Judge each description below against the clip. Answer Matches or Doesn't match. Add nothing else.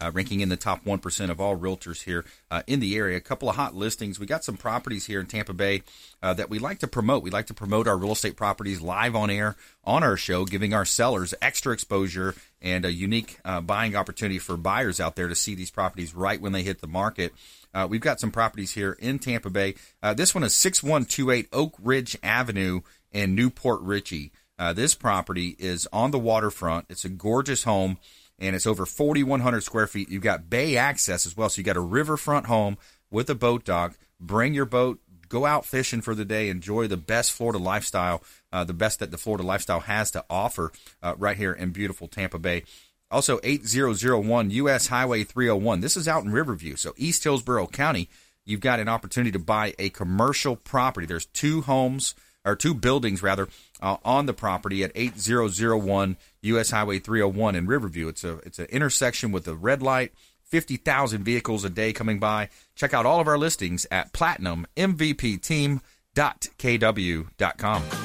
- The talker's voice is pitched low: Matches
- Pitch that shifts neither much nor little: Matches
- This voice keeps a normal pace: Matches